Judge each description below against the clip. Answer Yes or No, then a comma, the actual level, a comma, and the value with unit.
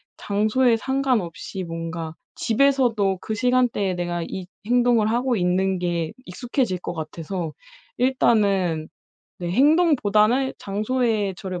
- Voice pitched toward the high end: Yes, high, 210 Hz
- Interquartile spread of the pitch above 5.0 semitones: Yes, wide, 5.6 semitones